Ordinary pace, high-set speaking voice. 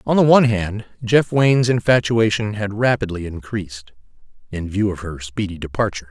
No: average, 155 wpm; low, 105 Hz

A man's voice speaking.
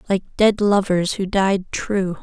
No: female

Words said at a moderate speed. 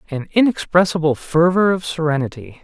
No: slow, 115 wpm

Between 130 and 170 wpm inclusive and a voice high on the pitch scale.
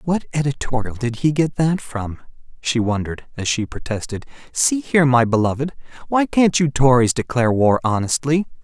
No: average, 160 wpm; low, 130 Hz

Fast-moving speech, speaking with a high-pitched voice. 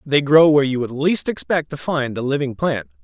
No: fast, 235 wpm; low, 135 Hz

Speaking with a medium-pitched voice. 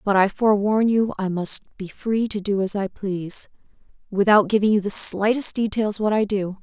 No: high, 205 Hz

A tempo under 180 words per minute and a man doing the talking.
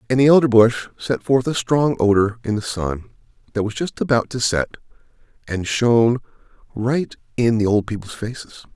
Yes: average, 170 wpm; male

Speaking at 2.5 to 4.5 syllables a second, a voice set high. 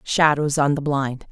No: 4.1 syllables/s; medium, 145 Hz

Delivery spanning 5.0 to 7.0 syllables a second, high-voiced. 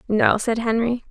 No: 4.4 syllables/s; high, 225 Hz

